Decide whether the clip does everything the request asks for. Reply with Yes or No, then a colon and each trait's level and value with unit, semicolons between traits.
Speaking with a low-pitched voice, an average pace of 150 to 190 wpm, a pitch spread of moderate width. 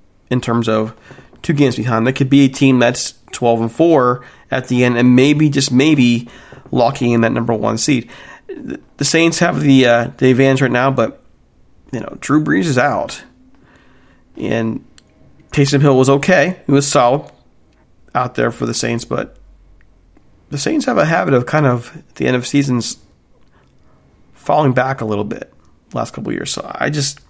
Yes: low, 130 Hz; average, 180 wpm; average, 3.1 semitones